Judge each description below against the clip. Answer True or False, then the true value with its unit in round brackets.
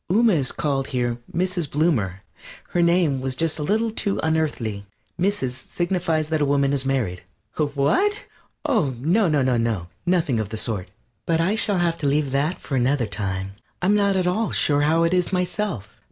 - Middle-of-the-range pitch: True (150 Hz)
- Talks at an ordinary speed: True (185 wpm)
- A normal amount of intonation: False (5.8 semitones)